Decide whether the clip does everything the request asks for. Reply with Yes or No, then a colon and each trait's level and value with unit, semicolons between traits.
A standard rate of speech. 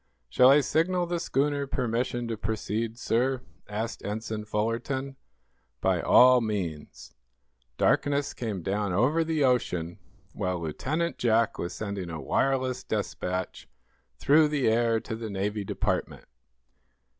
No: slow, 125 wpm